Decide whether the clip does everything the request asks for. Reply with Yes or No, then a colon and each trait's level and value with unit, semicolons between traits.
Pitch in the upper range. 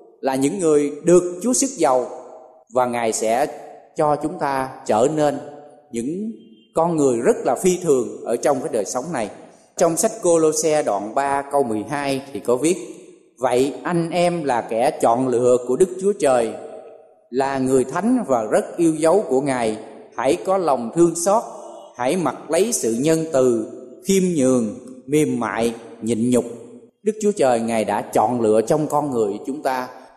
No: medium, 140 Hz